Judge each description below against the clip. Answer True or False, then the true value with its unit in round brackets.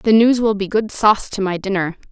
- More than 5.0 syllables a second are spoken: True (5.6 syllables/s)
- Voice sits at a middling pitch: False (205 Hz)